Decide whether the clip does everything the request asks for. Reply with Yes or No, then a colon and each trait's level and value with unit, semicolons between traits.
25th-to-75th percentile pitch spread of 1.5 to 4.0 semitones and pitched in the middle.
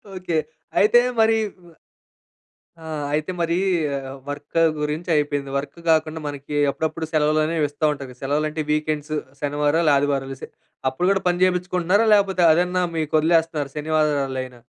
Yes: average, 2.8 semitones; medium, 155 Hz